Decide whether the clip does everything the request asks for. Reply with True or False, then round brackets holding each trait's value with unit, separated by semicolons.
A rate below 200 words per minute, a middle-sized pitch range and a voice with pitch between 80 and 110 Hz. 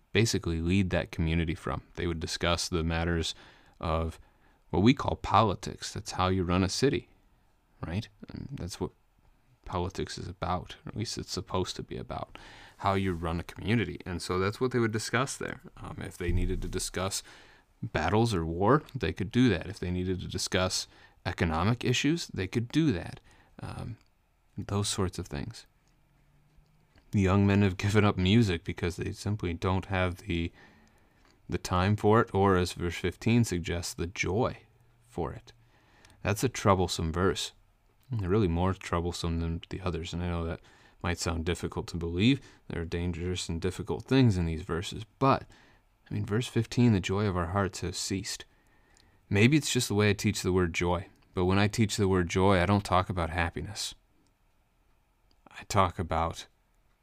True (180 wpm; 3.2 semitones; 95 Hz)